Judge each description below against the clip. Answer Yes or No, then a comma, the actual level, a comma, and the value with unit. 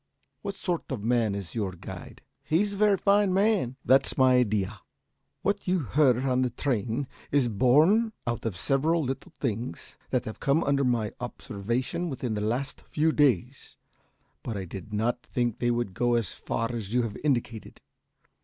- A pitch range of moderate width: Yes, average, 4.6 semitones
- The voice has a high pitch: No, low, 125 Hz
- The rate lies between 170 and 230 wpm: Yes, average, 175 wpm